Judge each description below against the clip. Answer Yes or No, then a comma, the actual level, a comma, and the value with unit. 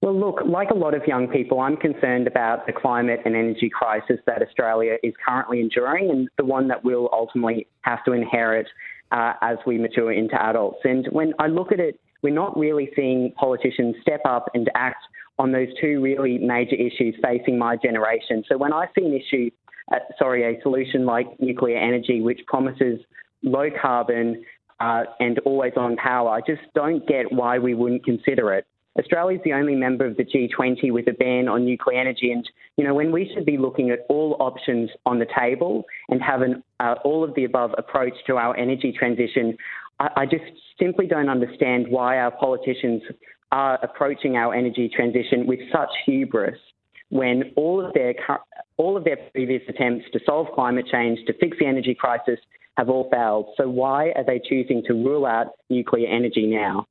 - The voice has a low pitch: Yes, low, 125 Hz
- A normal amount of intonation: No, narrow, 2.3 semitones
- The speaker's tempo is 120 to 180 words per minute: No, average, 190 wpm